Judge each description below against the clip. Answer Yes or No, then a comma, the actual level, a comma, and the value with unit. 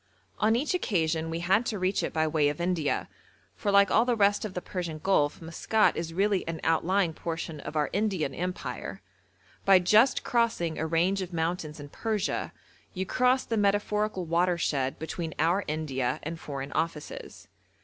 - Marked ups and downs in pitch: No, average, 4.0 semitones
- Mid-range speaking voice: Yes, medium, 175 Hz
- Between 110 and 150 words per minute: No, average, 170 wpm